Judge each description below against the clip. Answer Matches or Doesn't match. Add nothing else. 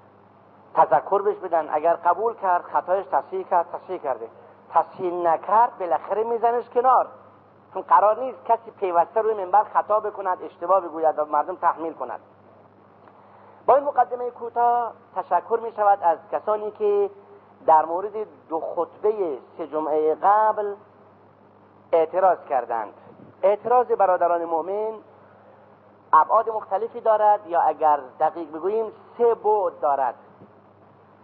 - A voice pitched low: Doesn't match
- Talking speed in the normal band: Matches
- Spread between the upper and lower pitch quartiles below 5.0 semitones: Doesn't match